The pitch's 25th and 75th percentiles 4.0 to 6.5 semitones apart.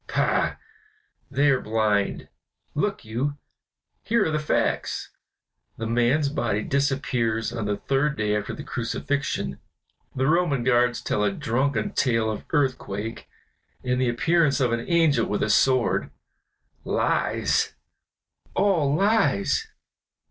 Yes: average, 4.8 semitones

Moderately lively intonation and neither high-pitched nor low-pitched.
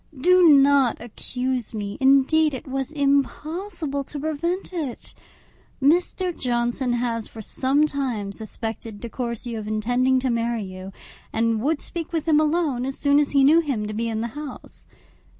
No: average, 4.4 semitones; very high, 265 Hz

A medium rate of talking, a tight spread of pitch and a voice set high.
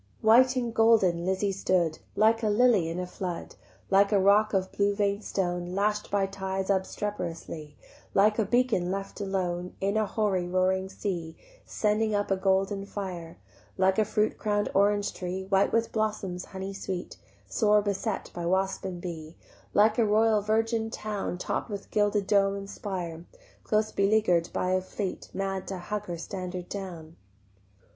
Yes: average, 165 wpm; narrow, 2.3 semitones; high, 195 Hz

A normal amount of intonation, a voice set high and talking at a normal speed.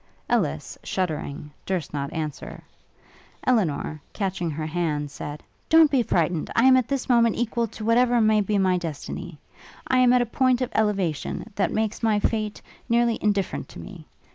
No: wide, 6.2 semitones; high, 210 Hz; average, 165 wpm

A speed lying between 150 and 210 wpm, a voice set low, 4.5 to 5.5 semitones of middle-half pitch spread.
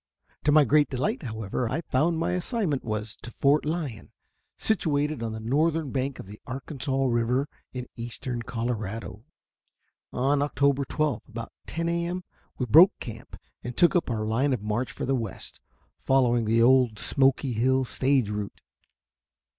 No: average, 160 wpm; low, 130 Hz; average, 4.1 semitones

